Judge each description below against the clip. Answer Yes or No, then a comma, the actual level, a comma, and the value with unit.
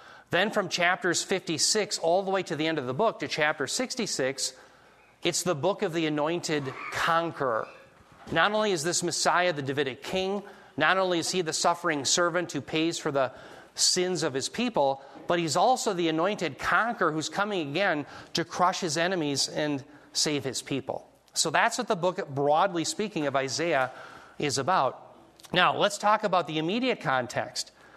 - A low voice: No, medium, 170 Hz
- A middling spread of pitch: Yes, average, 4.1 semitones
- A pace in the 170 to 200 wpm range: Yes, average, 175 wpm